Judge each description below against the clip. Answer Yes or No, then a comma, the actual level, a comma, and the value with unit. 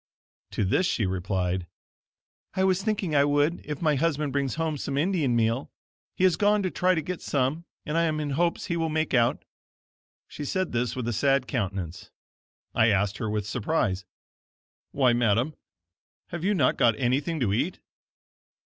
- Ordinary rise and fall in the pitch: No, wide, 6.3 semitones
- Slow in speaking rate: No, average, 175 wpm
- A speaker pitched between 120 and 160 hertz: Yes, medium, 140 Hz